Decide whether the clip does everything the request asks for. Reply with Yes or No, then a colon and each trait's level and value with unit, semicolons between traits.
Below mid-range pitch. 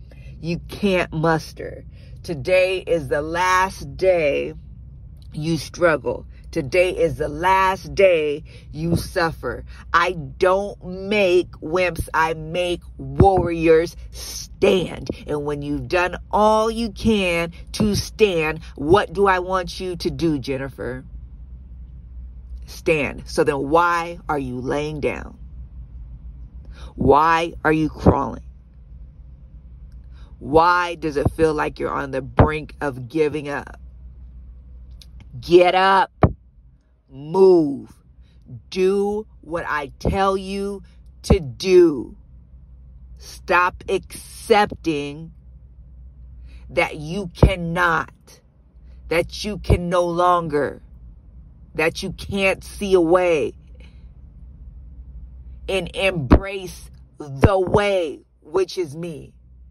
No: medium, 150 Hz